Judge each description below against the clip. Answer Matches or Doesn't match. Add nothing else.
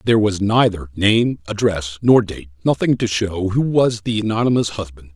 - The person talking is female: Doesn't match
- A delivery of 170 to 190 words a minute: Matches